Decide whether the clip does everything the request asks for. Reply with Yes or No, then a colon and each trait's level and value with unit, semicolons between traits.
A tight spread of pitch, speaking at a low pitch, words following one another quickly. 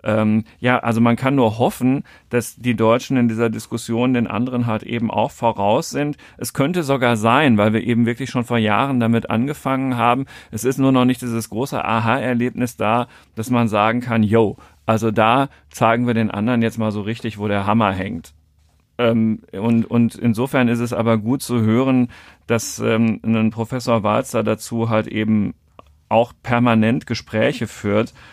No: narrow, 1.9 semitones; low, 115 Hz; average, 180 wpm